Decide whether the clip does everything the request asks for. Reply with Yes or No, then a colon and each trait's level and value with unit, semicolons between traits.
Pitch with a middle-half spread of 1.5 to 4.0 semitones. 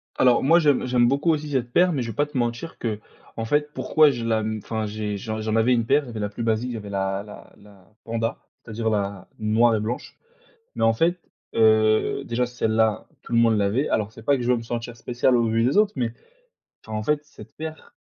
Yes: average, 2.8 semitones